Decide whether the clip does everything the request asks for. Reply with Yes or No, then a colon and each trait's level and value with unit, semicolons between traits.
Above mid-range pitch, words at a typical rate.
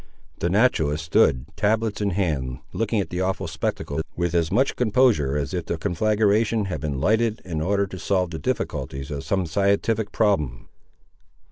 No: very low, 95 Hz; average, 165 wpm